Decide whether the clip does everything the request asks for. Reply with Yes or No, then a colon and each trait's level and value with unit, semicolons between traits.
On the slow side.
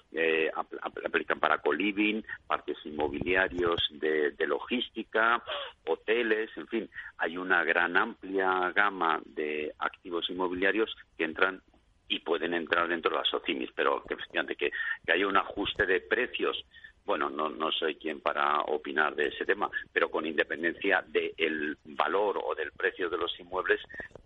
No: average, 155 wpm